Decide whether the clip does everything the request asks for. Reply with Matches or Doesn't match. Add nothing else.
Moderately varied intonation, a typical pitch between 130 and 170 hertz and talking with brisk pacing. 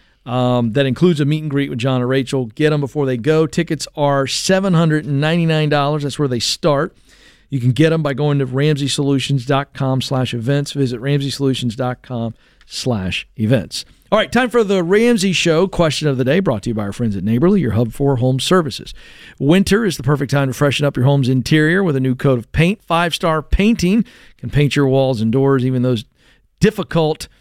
Matches